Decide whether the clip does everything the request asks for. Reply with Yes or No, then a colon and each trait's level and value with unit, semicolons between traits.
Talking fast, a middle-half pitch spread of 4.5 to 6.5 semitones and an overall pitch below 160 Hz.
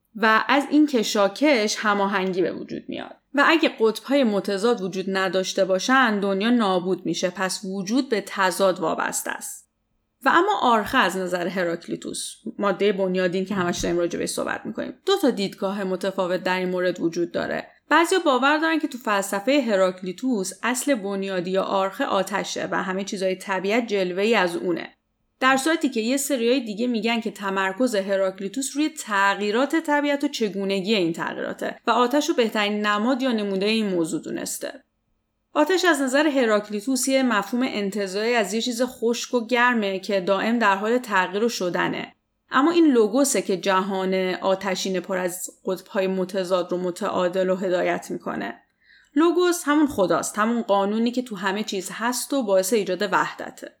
No: fast, 160 wpm; average, 5.1 semitones; high, 205 Hz